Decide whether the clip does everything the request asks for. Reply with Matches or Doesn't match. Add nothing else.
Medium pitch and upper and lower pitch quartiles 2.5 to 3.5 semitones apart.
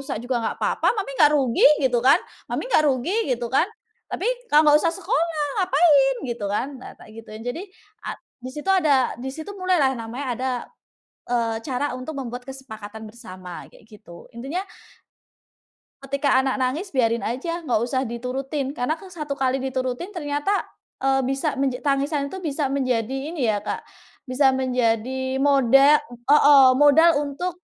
Doesn't match